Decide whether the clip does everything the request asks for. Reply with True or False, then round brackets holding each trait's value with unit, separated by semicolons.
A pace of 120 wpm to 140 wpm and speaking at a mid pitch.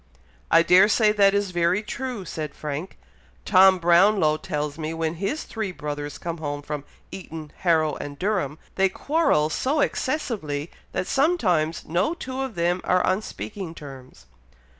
False (155 wpm; 175 Hz)